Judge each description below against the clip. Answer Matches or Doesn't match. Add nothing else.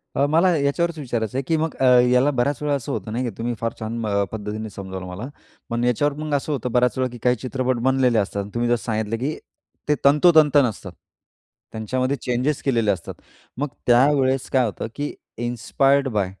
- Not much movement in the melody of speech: Doesn't match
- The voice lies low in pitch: Matches